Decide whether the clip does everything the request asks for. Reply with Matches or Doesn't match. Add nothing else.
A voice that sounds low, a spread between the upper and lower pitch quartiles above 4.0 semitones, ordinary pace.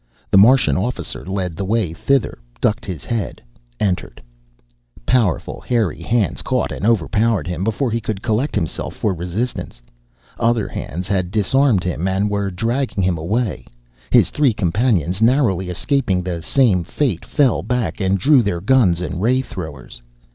Matches